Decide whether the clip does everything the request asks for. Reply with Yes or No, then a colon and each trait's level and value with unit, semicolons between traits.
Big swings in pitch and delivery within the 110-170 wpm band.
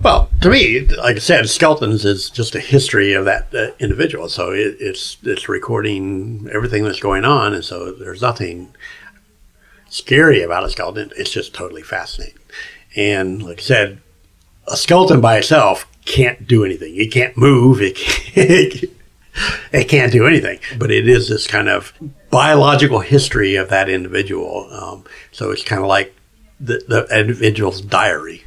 Yes: wide, 6.1 semitones; average, 160 wpm